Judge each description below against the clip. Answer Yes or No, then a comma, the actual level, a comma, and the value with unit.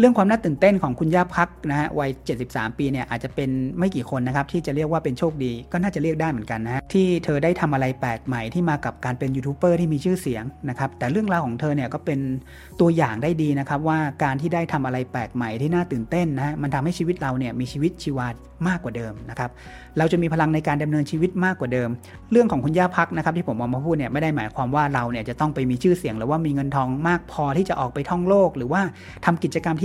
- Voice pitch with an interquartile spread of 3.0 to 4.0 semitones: No, average, 4.7 semitones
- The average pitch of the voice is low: No, medium, 150 Hz